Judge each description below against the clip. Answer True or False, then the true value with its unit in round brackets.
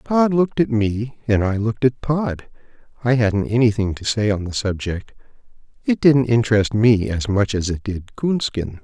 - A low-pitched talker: True (115 Hz)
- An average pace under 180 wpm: False (185 wpm)